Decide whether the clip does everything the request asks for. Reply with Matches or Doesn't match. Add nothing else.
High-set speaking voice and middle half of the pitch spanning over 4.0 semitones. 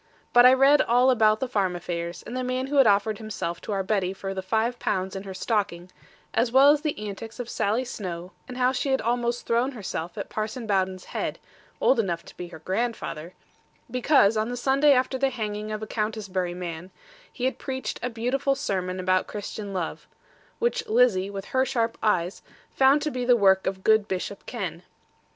Matches